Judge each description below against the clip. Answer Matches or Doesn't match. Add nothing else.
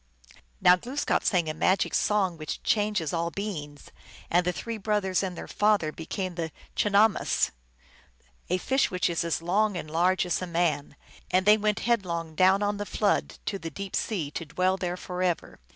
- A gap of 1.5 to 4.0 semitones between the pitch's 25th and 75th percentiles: Matches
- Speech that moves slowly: Doesn't match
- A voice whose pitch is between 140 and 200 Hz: Matches